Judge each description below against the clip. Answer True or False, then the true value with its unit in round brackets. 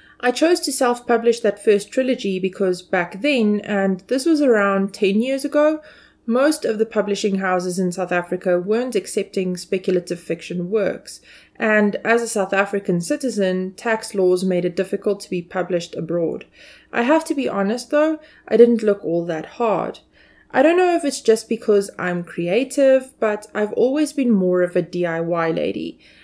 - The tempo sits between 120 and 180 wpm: True (170 wpm)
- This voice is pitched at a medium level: False (205 Hz)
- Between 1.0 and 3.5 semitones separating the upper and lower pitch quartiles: False (5.1 semitones)